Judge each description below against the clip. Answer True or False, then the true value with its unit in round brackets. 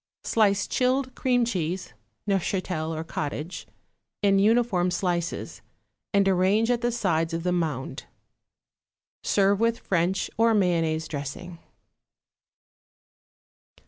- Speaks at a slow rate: True (105 wpm)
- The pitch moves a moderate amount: True (4.8 semitones)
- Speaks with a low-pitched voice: False (185 Hz)